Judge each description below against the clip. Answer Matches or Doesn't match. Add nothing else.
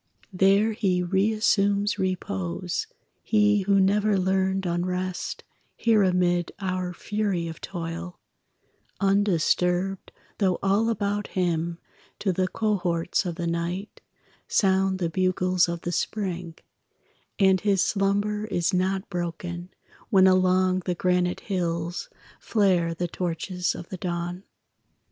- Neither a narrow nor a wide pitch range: Doesn't match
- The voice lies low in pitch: Doesn't match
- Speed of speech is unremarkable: Doesn't match